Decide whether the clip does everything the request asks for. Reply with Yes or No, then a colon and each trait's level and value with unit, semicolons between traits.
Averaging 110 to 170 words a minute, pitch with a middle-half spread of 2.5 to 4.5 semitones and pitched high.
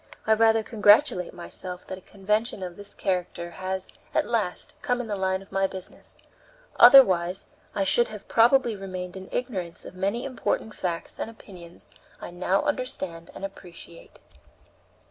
Yes: average, 155 wpm; average, 3.5 semitones; high, 195 Hz